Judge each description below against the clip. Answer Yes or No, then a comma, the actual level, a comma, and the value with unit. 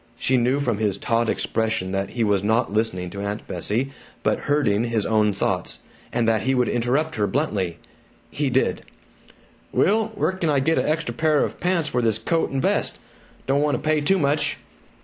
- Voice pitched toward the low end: Yes, low, 120 Hz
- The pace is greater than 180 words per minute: Yes, average, 195 wpm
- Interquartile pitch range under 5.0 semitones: No, wide, 5.5 semitones